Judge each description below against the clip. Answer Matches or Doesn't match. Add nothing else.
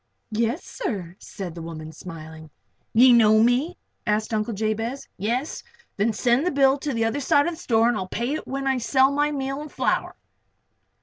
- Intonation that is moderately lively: Matches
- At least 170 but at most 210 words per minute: Matches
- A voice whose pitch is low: Doesn't match